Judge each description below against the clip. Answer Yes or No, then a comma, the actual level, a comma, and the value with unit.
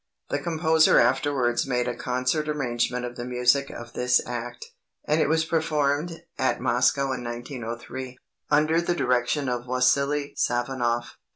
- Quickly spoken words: No, average, 145 wpm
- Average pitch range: Yes, average, 3.2 semitones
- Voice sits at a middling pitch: No, low, 130 Hz